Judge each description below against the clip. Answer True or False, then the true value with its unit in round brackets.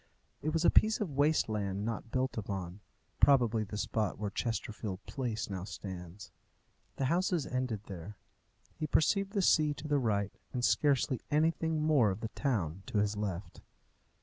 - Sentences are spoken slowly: False (165 wpm)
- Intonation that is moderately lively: False (6.4 semitones)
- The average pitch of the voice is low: True (115 Hz)